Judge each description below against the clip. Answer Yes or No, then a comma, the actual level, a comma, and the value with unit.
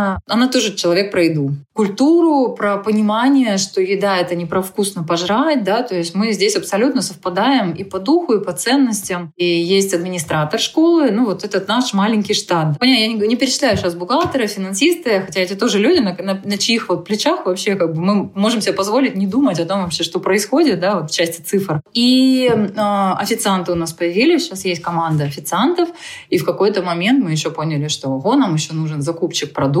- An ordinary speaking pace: No, fast, 195 wpm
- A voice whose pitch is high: Yes, high, 200 Hz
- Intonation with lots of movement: Yes, wide, 5.7 semitones